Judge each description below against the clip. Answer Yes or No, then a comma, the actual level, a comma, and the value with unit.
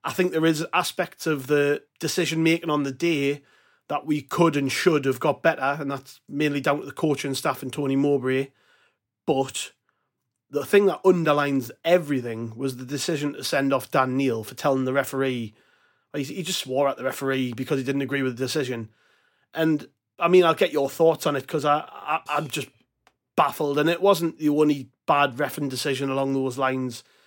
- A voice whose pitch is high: No, medium, 140 Hz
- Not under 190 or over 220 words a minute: Yes, average, 195 wpm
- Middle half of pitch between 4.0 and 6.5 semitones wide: No, average, 2.8 semitones